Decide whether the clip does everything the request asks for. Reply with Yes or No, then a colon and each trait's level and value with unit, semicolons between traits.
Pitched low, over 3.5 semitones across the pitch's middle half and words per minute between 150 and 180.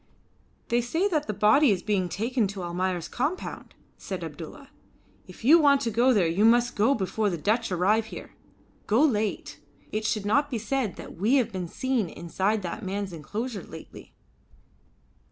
No: high, 215 Hz; average, 4.5 semitones; average, 170 wpm